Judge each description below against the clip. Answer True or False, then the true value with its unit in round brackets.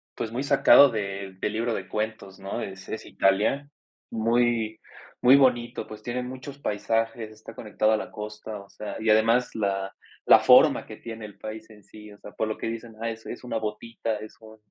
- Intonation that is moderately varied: False (1.6 semitones)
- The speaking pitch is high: False (110 Hz)